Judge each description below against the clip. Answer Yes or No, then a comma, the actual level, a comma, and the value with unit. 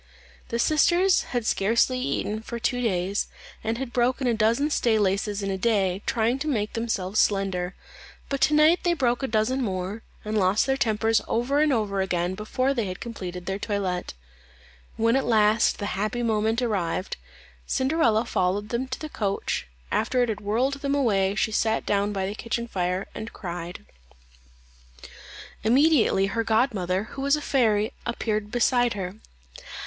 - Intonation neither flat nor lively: Yes, average, 3.8 semitones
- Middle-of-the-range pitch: No, high, 220 Hz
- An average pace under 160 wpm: No, average, 165 wpm